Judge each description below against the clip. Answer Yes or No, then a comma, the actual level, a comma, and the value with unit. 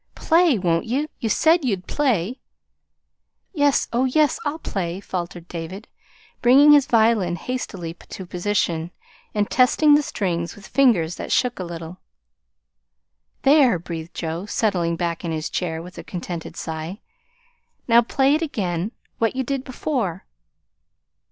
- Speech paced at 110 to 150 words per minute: Yes, average, 140 wpm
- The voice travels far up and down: Yes, wide, 7.1 semitones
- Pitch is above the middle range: Yes, high, 200 Hz